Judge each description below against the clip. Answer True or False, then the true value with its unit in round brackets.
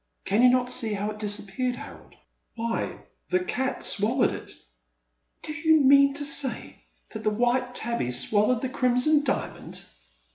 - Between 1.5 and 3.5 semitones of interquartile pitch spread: False (4.3 semitones)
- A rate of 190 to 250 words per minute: False (160 wpm)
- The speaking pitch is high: True (245 Hz)